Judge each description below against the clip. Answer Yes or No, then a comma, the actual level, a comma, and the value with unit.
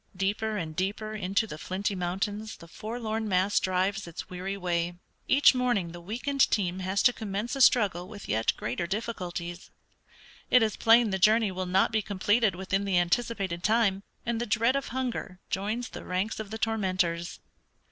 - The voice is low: No, high, 200 Hz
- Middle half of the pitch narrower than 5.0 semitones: Yes, average, 3.4 semitones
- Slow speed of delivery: No, average, 175 wpm